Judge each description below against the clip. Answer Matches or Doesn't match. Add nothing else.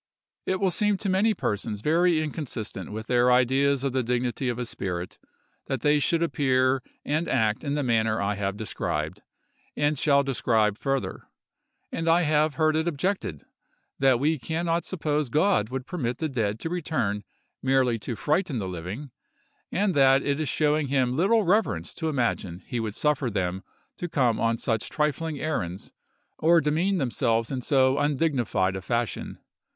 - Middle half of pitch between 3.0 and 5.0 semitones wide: Doesn't match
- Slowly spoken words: Doesn't match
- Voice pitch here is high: Doesn't match